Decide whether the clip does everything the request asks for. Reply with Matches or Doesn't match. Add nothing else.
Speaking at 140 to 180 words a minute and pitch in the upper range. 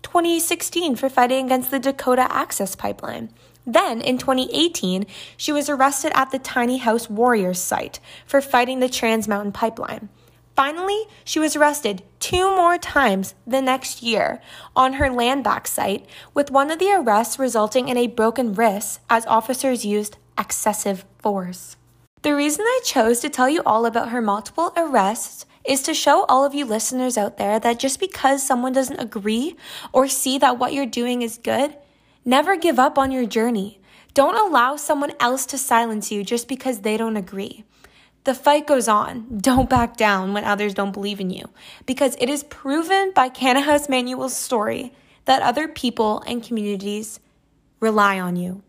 Matches